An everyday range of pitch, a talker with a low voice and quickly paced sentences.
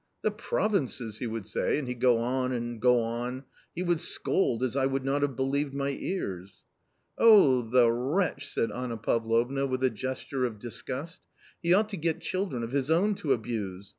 Yes: average, 3.6 semitones; low, 130 Hz; fast, 210 wpm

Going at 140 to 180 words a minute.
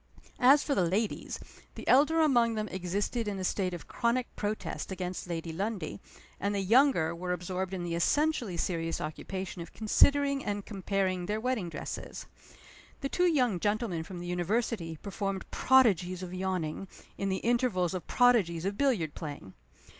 Yes: average, 160 wpm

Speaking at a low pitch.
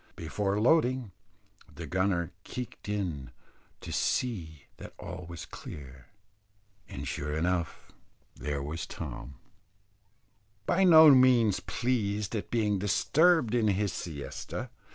Yes: low, 100 Hz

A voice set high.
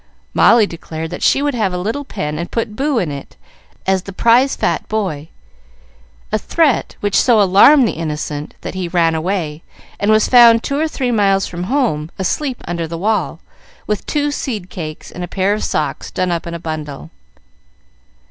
Yes: high, 195 Hz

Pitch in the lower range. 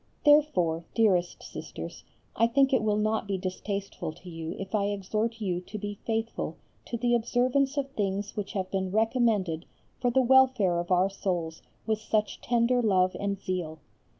No: high, 205 Hz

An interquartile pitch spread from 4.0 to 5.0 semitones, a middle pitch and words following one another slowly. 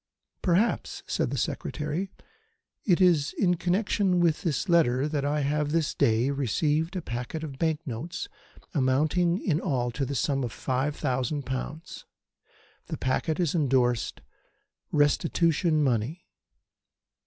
Yes: average, 4.3 semitones; medium, 150 Hz; slow, 130 wpm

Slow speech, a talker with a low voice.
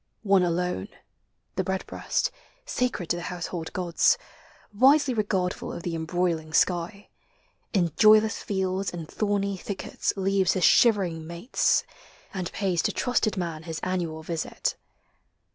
No: slow, 125 wpm; medium, 185 Hz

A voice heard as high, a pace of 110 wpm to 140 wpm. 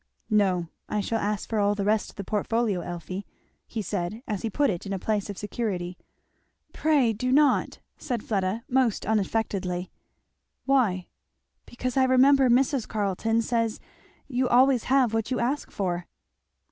No: high, 220 Hz; average, 160 wpm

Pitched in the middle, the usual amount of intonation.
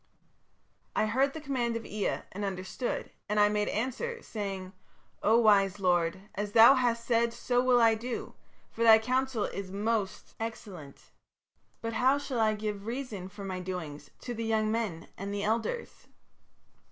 No: high, 220 Hz; average, 3.1 semitones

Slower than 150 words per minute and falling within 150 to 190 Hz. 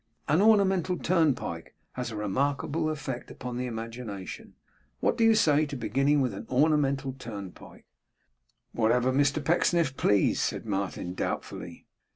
No: slow, 135 wpm; low, 135 Hz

